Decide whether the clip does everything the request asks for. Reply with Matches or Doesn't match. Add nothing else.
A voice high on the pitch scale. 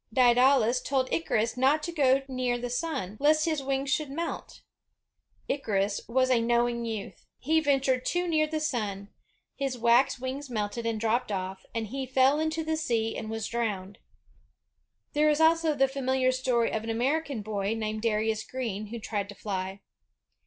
Matches